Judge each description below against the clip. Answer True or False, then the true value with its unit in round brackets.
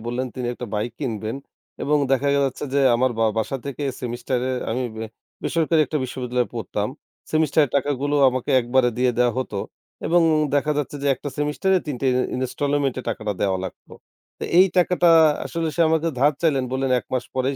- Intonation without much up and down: False (3.2 semitones)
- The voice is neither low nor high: False (130 Hz)